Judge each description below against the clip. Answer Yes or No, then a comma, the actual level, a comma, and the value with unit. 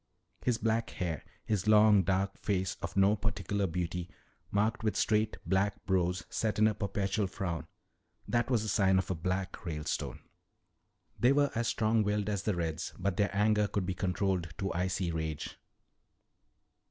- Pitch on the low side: Yes, low, 100 Hz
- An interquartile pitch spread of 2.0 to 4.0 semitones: Yes, average, 2.9 semitones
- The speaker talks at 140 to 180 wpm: Yes, average, 165 wpm